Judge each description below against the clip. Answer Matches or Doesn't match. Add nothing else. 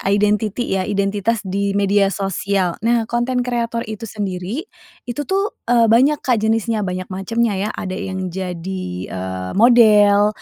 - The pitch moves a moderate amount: Matches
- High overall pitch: Matches